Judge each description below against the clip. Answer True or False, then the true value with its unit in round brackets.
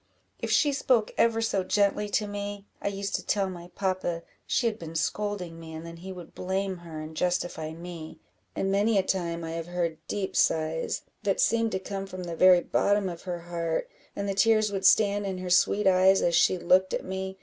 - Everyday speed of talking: False (215 wpm)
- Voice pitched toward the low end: False (185 Hz)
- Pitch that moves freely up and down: False (2.9 semitones)